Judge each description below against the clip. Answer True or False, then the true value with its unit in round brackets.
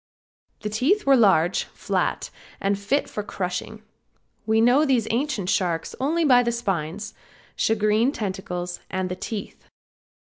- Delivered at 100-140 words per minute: True (135 wpm)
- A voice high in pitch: True (215 Hz)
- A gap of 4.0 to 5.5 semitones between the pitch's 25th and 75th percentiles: True (4.7 semitones)